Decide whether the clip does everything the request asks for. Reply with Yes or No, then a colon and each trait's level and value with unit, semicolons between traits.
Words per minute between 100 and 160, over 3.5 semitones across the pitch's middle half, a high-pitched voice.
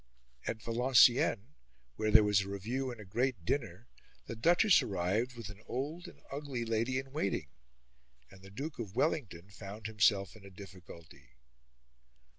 No: average, 155 wpm; average, 4.7 semitones; low, 110 Hz